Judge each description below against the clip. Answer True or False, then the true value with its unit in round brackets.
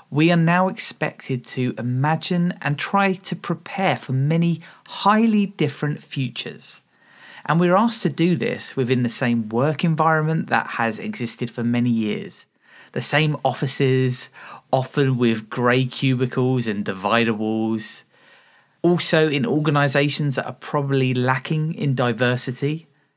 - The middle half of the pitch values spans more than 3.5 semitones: True (4.7 semitones)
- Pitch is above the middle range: False (140 Hz)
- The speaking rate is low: True (130 wpm)